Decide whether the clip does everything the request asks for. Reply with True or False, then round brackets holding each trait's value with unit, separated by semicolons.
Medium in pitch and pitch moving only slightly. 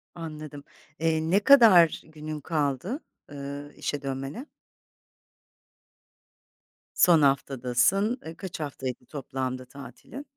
False (150 Hz; 3.6 semitones)